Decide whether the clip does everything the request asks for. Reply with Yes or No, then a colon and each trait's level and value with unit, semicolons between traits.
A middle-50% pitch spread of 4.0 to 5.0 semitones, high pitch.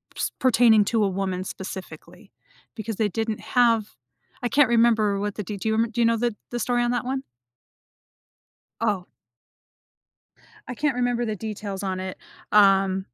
No: average, 3.5 semitones; high, 220 Hz